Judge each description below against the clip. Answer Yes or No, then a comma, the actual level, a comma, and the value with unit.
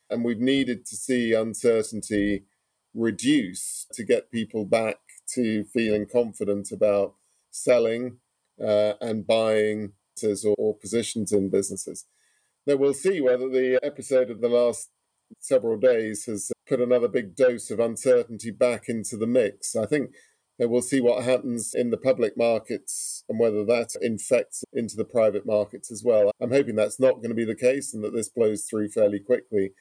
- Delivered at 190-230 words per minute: No, average, 165 wpm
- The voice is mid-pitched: No, low, 115 Hz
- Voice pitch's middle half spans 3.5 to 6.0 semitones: No, average, 2.8 semitones